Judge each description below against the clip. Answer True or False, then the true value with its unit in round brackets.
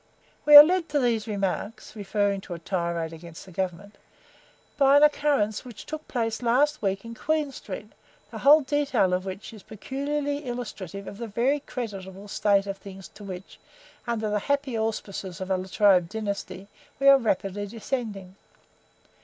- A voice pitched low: False (215 Hz)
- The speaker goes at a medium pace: True (170 wpm)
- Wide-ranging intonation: True (5.8 semitones)